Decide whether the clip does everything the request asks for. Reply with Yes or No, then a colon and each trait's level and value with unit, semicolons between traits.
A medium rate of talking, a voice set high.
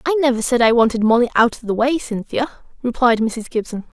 No: fast, 210 wpm; high, 240 Hz